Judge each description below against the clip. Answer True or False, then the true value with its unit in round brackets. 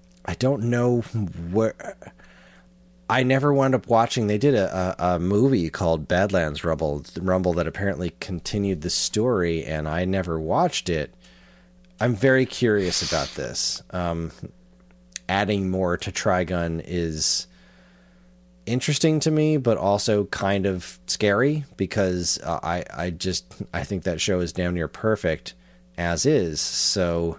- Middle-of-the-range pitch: False (90 Hz)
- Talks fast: False (140 wpm)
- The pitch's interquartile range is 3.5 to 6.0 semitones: True (4.9 semitones)